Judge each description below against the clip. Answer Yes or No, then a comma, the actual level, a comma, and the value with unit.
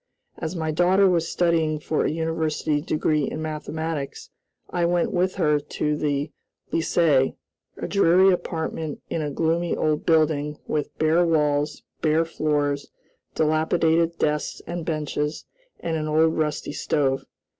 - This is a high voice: No, medium, 155 Hz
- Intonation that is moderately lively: No, narrow, 1.7 semitones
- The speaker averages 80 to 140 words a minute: Yes, slow, 135 wpm